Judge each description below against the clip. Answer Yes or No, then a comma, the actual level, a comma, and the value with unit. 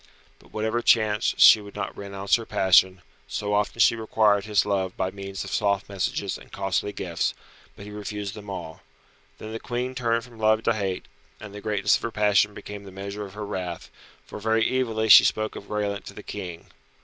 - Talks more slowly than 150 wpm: No, fast, 205 wpm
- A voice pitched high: No, low, 105 Hz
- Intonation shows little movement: Yes, narrow, 1.9 semitones